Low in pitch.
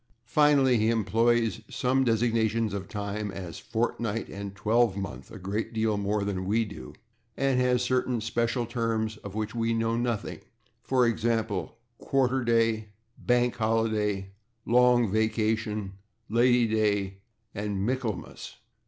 Yes: low, 115 Hz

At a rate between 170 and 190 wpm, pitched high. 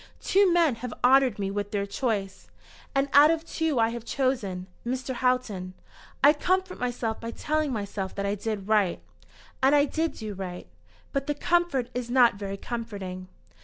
Yes: average, 175 wpm; high, 240 Hz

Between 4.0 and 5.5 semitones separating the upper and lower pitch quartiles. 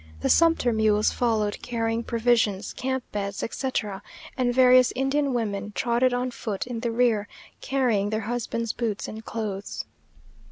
No: average, 2.8 semitones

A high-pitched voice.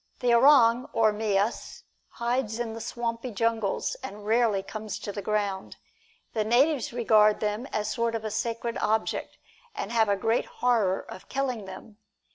Yes: high, 225 Hz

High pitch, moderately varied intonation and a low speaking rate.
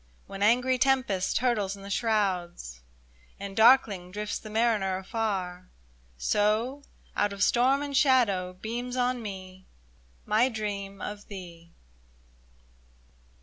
Yes: high, 210 Hz; average, 4.1 semitones; slow, 115 wpm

